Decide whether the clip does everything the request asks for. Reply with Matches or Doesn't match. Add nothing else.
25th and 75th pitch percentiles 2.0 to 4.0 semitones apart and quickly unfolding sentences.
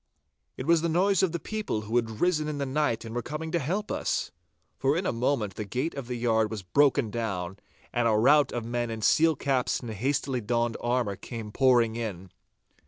Doesn't match